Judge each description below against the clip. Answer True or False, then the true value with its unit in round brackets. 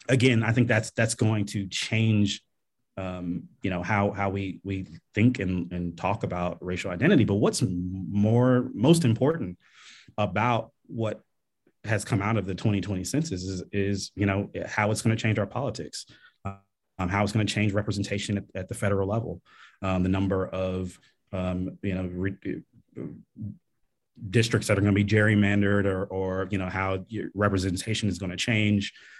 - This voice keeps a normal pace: True (175 wpm)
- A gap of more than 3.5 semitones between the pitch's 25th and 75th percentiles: False (2.6 semitones)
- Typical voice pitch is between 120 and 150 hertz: False (100 Hz)